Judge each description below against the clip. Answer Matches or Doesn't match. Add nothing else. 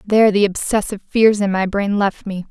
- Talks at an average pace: Doesn't match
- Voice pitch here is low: Doesn't match